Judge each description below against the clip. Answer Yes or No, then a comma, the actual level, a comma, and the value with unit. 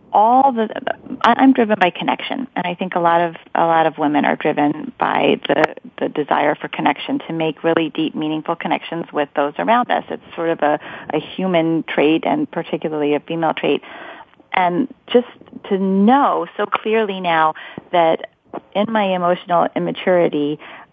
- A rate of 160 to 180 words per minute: Yes, average, 165 wpm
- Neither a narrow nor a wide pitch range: No, wide, 6.0 semitones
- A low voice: No, medium, 175 Hz